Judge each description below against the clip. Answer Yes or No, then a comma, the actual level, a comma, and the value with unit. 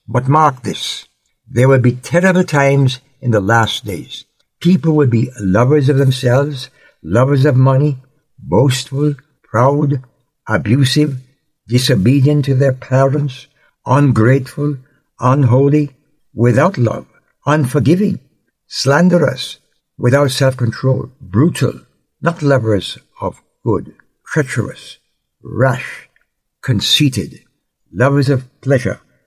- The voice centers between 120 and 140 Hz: Yes, low, 135 Hz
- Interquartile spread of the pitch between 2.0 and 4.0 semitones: Yes, narrow, 2.4 semitones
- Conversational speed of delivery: No, slow, 95 wpm